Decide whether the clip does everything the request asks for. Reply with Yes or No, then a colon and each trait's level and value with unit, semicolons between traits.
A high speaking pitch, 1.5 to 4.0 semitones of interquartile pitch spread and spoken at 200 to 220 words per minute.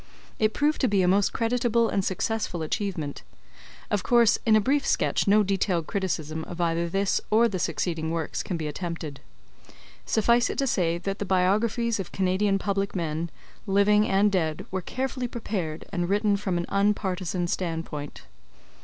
No: high, 195 Hz; average, 3.7 semitones; average, 170 wpm